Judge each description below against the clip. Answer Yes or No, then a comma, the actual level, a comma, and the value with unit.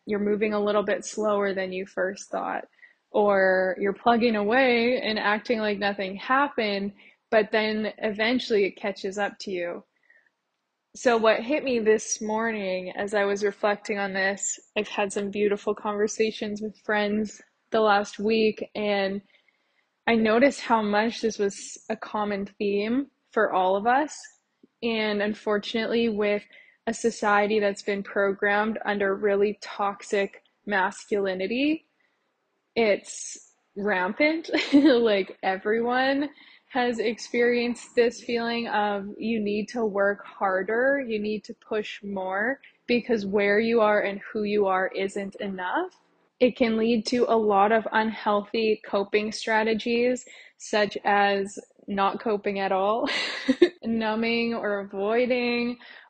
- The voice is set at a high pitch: Yes, high, 215 Hz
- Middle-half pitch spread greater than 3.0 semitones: No, narrow, 2.6 semitones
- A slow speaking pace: Yes, slow, 130 wpm